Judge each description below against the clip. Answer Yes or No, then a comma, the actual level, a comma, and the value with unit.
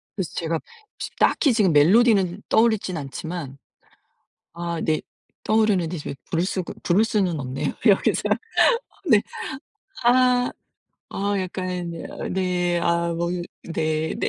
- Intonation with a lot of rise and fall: No, average, 3.6 semitones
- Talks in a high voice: No, medium, 180 Hz